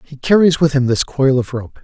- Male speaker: Yes, male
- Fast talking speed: Yes, fast, 260 wpm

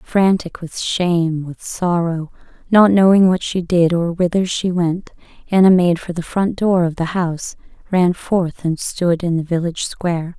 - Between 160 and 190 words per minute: Yes, average, 180 wpm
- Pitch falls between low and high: Yes, medium, 175 Hz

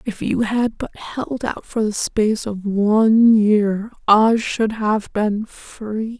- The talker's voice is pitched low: No, high, 215 Hz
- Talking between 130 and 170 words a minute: Yes, average, 165 wpm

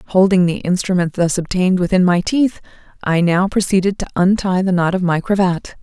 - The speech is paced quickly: No, average, 185 wpm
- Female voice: Yes, female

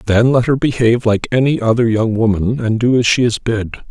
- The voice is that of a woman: No, male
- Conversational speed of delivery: No, fast, 230 wpm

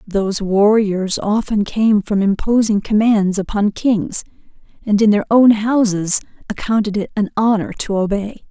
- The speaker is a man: No, female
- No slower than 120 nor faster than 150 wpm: Yes, average, 140 wpm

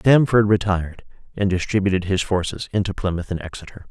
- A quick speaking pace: No, average, 155 wpm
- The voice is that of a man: Yes, male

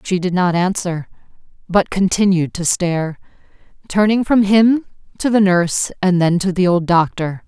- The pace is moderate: Yes, average, 160 wpm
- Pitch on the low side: No, medium, 185 Hz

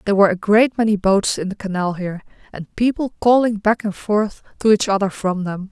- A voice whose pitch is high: Yes, high, 205 Hz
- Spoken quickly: Yes, fast, 220 wpm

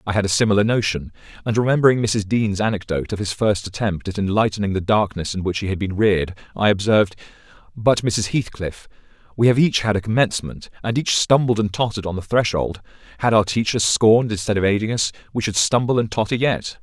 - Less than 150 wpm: No, average, 200 wpm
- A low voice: Yes, low, 105 Hz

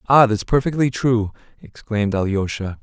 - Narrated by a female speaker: No, male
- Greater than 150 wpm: No, slow, 125 wpm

